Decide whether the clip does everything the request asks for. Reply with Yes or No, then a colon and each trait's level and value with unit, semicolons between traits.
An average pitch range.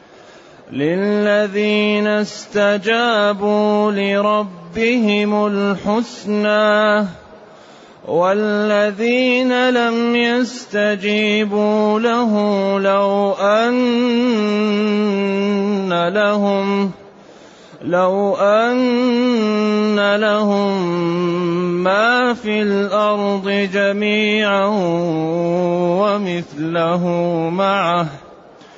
No: narrow, 1.2 semitones